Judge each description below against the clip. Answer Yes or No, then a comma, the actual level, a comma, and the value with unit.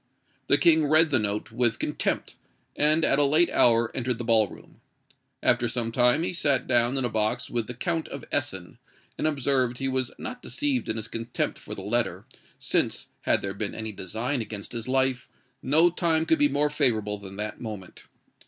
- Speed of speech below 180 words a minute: No, average, 195 wpm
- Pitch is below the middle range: Yes, low, 125 Hz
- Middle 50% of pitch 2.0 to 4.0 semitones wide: No, average, 4.9 semitones